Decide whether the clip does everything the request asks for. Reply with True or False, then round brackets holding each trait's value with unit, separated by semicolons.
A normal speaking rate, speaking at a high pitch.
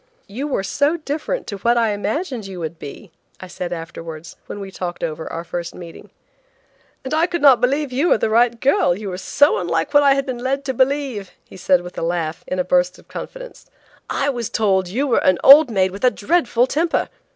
False (225 wpm; 220 Hz)